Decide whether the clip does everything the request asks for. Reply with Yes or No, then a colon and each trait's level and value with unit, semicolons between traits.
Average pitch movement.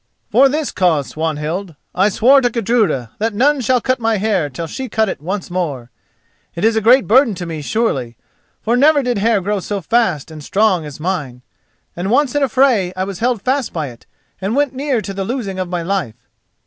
No: wide, 6.4 semitones